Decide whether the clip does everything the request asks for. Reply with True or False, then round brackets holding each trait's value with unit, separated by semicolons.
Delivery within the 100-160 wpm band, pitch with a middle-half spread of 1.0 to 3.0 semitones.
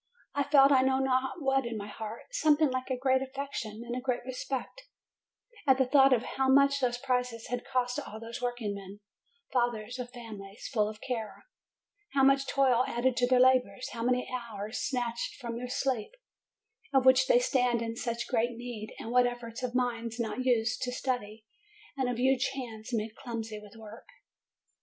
False (185 wpm; 2.4 semitones)